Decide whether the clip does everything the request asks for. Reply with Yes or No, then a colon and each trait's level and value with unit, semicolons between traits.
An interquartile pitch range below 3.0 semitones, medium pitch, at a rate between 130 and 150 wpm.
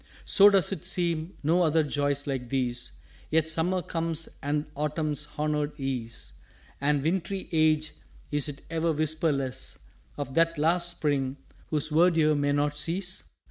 Yes: narrow, 2.5 semitones; medium, 155 Hz; average, 140 wpm